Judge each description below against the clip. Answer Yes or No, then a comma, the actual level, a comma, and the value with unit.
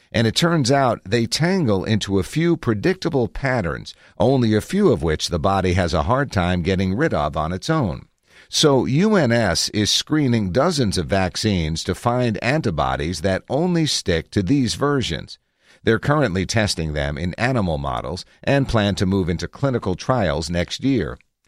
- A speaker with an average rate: Yes, average, 170 wpm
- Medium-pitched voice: No, low, 105 Hz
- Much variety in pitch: Yes, wide, 6.6 semitones